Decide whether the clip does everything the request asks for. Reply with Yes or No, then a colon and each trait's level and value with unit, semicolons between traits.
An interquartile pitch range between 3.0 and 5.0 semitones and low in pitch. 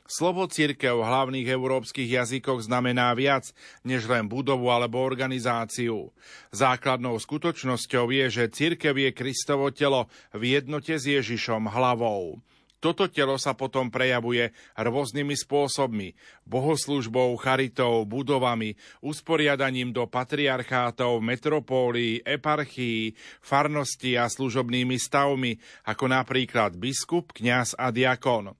No: narrow, 2.4 semitones; low, 130 Hz